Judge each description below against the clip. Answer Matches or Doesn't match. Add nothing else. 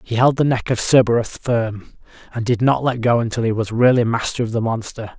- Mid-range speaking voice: Doesn't match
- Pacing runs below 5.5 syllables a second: Doesn't match